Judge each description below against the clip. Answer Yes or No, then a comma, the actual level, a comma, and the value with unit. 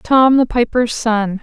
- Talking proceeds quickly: No, average, 170 wpm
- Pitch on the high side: Yes, high, 235 Hz